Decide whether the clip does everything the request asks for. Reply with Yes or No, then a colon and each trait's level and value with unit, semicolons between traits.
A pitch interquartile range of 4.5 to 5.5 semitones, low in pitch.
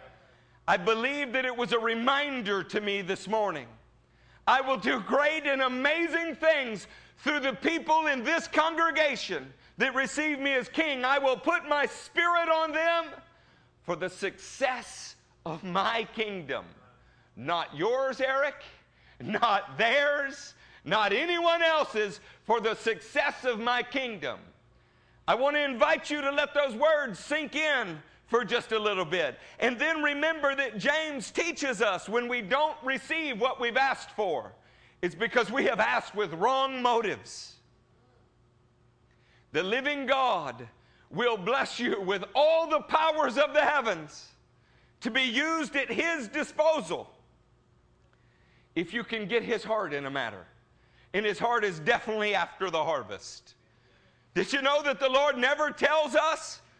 No: average, 4.8 semitones; very high, 270 Hz